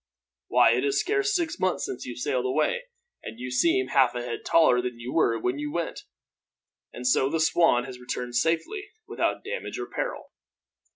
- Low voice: Yes, low, 130 Hz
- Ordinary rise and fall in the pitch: No, wide, 7.0 semitones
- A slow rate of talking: No, average, 185 wpm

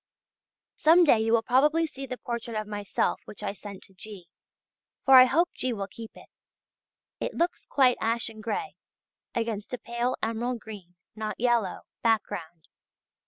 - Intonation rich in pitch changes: No, average, 3.3 semitones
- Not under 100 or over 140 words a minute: No, average, 160 wpm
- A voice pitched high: Yes, high, 230 Hz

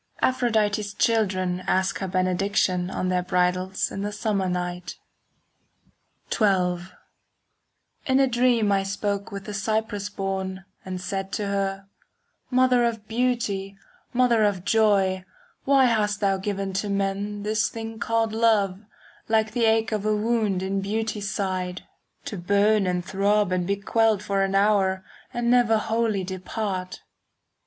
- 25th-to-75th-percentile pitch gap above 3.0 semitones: No, narrow, 2.6 semitones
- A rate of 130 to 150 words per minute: Yes, average, 145 wpm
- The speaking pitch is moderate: No, high, 200 Hz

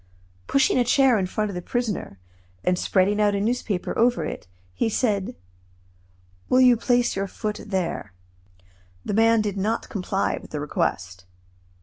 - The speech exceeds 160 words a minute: No, average, 150 wpm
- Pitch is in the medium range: No, high, 210 Hz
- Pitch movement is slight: No, average, 4.3 semitones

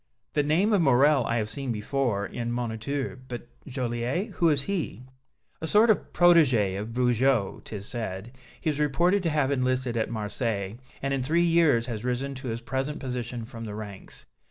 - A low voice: Yes, low, 125 Hz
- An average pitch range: Yes, average, 4.3 semitones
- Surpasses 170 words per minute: Yes, average, 185 wpm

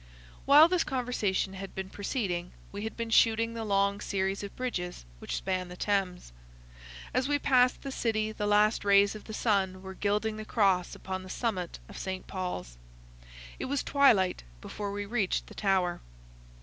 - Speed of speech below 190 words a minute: Yes, average, 175 wpm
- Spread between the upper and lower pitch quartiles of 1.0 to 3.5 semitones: Yes, average, 3.1 semitones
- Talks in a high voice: Yes, high, 205 Hz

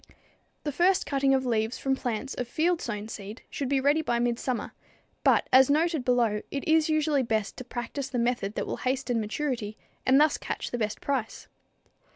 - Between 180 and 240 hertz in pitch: No, very high, 255 Hz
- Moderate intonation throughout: Yes, average, 3.5 semitones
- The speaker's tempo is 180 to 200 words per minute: Yes, average, 190 wpm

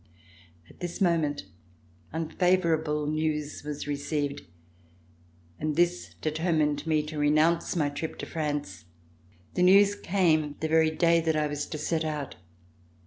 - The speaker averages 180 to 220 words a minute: No, average, 140 wpm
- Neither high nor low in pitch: Yes, medium, 155 Hz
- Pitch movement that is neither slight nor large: No, narrow, 2.1 semitones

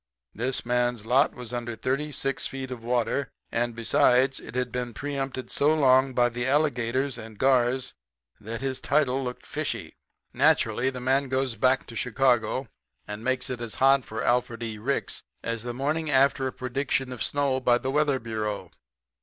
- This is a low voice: Yes, low, 125 Hz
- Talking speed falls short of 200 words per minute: Yes, average, 170 wpm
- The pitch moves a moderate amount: No, narrow, 2.2 semitones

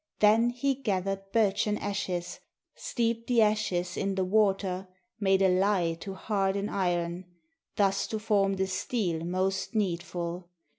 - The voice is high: Yes, high, 195 Hz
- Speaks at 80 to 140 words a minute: Yes, slow, 135 wpm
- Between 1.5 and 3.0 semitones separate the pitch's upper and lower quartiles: Yes, narrow, 2.5 semitones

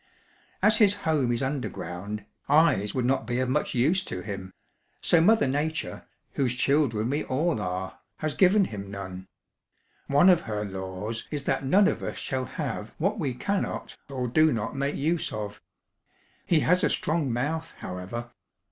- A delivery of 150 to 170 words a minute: Yes, average, 165 wpm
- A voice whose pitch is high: No, low, 130 Hz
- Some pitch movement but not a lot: No, wide, 6.9 semitones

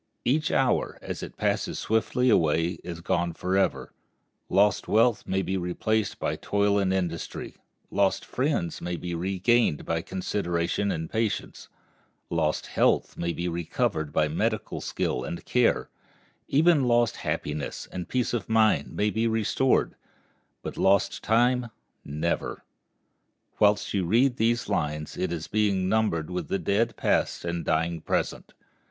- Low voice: Yes, very low, 95 Hz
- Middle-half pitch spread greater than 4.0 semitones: Yes, average, 4.8 semitones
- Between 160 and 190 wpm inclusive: No, average, 140 wpm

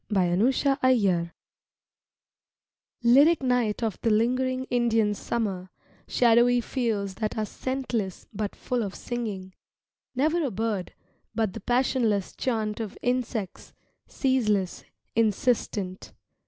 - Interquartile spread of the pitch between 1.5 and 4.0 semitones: Yes, average, 3.7 semitones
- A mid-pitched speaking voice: No, high, 225 Hz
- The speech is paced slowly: Yes, slow, 110 wpm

